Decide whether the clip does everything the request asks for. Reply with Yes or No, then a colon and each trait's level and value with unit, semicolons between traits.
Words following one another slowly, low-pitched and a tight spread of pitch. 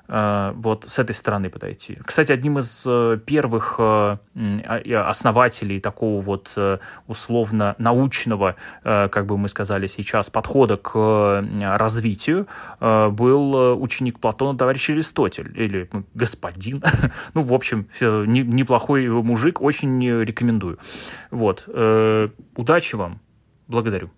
No: slow, 95 wpm; low, 115 Hz; average, 3.5 semitones